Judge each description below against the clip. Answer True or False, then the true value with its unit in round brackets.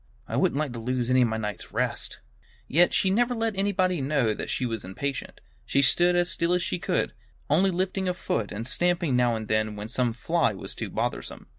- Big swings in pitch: True (7.7 semitones)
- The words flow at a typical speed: False (220 wpm)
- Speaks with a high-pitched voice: False (140 Hz)